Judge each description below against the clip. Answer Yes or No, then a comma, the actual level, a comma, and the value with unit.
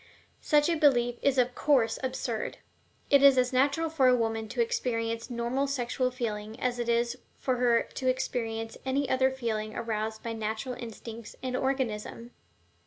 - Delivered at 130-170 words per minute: Yes, average, 165 wpm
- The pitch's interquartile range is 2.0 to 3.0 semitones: Yes, narrow, 2.5 semitones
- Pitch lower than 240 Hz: No, high, 245 Hz